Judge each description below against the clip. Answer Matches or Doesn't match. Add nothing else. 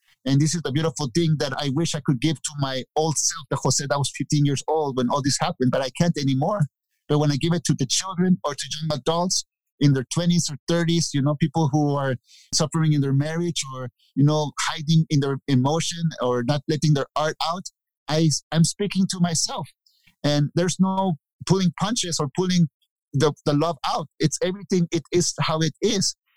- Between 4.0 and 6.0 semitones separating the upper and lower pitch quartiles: Doesn't match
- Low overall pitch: Doesn't match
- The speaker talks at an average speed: Doesn't match